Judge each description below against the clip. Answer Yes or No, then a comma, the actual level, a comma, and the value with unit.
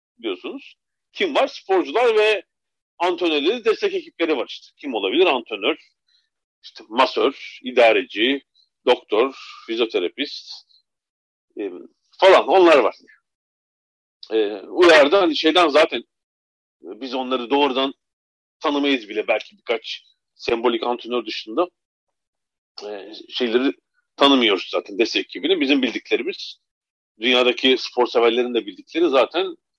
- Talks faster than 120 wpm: No, average, 105 wpm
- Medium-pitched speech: No, very high, 275 Hz